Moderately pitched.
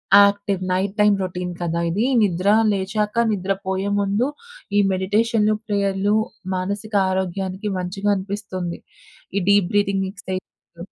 No: high, 195 Hz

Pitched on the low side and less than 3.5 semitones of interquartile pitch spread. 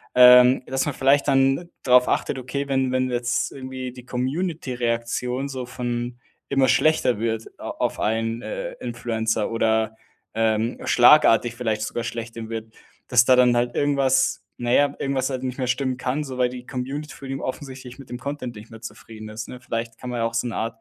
Yes: low, 125 Hz; narrow, 2.4 semitones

